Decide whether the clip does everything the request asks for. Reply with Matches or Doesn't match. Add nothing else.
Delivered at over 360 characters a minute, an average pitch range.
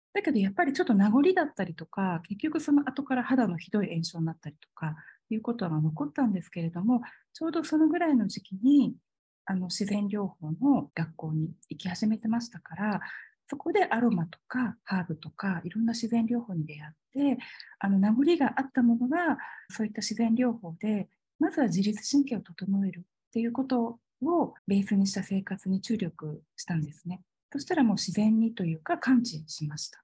Doesn't match